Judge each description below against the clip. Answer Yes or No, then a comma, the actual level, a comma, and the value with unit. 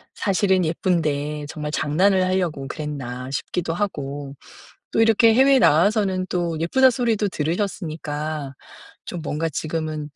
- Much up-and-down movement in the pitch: No, average, 4.6 semitones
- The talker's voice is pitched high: No, medium, 165 Hz